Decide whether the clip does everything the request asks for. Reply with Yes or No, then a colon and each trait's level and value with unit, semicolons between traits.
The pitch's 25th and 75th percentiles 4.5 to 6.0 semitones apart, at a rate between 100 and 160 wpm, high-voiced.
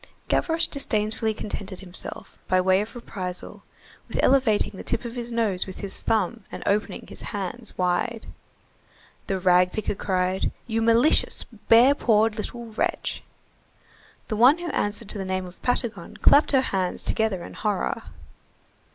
No: average, 3.8 semitones; average, 150 wpm; high, 215 Hz